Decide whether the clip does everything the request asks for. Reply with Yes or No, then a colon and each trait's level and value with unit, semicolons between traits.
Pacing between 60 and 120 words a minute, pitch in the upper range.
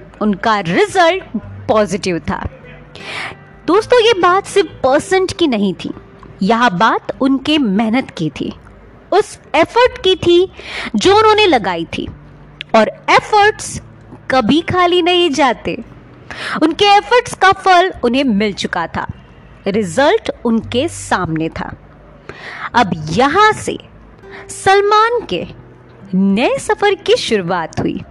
Yes: average, 115 wpm; very high, 290 Hz